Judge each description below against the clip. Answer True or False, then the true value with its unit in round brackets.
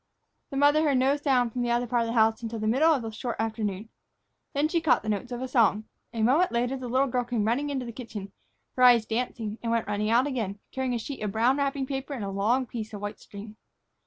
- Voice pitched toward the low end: False (240 Hz)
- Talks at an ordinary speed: False (255 wpm)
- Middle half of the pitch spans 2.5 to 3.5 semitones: True (3.2 semitones)